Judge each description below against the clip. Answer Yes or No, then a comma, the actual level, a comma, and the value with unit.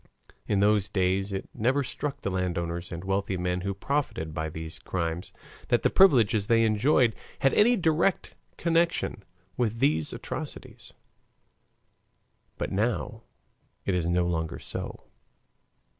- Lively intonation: Yes, wide, 5.8 semitones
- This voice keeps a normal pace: No, slow, 130 wpm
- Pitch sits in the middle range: No, low, 100 Hz